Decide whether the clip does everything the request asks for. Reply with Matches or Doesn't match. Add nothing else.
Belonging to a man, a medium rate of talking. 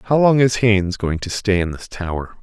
Doesn't match